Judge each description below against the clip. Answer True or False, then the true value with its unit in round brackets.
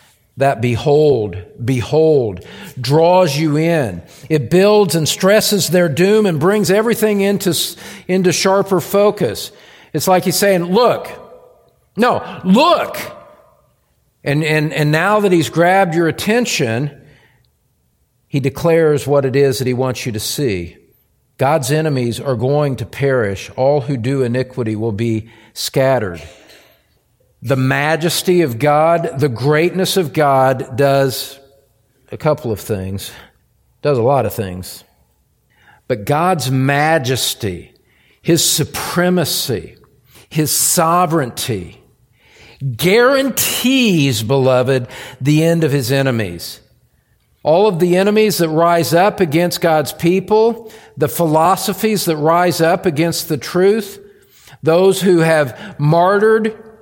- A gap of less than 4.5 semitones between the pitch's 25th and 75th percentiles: False (5.6 semitones)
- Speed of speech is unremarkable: False (120 wpm)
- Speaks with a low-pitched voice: False (155 Hz)